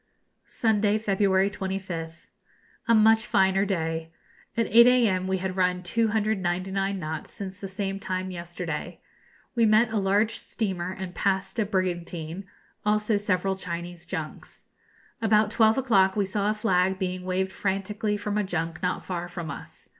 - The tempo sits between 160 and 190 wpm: No, average, 150 wpm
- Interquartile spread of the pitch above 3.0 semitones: No, narrow, 2.5 semitones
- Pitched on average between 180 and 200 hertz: Yes, high, 190 Hz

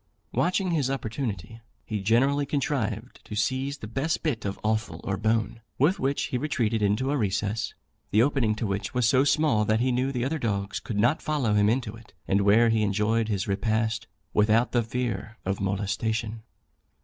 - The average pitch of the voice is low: Yes, low, 115 Hz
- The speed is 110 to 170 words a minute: No, average, 185 wpm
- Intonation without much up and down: No, average, 3.8 semitones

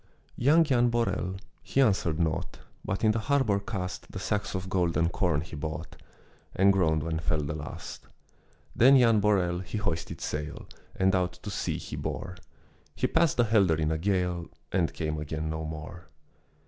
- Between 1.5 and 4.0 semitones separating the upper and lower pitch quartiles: No, average, 4.8 semitones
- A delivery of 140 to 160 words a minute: No, average, 175 wpm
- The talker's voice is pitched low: Yes, very low, 90 Hz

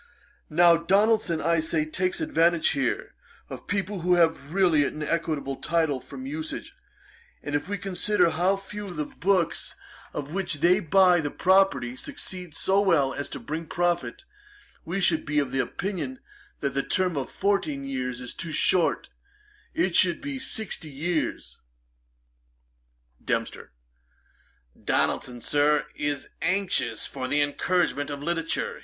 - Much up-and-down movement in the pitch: No, average, 4.6 semitones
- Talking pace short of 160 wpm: Yes, average, 140 wpm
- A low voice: No, medium, 170 Hz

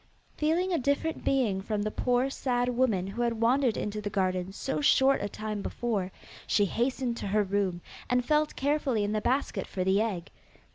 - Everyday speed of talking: Yes, average, 190 wpm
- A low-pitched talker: No, high, 230 Hz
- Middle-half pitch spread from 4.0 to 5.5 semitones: Yes, average, 4.6 semitones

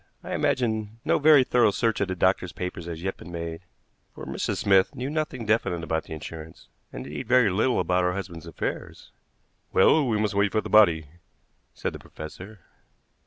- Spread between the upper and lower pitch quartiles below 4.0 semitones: No, average, 5.0 semitones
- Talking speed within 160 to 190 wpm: Yes, average, 185 wpm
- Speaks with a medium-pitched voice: No, very low, 95 Hz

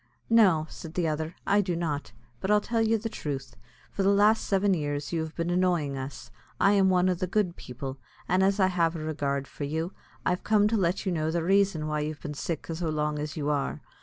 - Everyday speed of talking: No, fast, 235 wpm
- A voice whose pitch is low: No, medium, 170 Hz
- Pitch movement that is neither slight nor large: Yes, average, 4.2 semitones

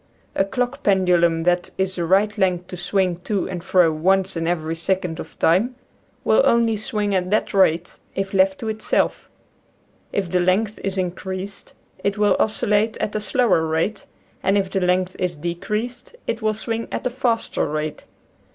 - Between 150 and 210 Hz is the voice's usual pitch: Yes, high, 190 Hz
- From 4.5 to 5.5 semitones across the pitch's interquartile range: No, average, 3.1 semitones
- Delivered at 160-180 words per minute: Yes, average, 175 wpm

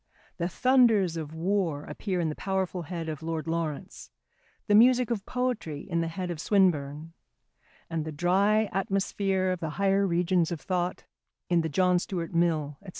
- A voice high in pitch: No, medium, 175 Hz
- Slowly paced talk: No, average, 170 wpm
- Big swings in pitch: No, average, 3.2 semitones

